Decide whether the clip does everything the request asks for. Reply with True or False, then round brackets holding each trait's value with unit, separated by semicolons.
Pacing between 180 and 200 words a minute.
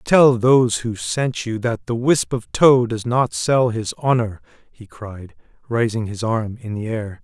True (190 wpm)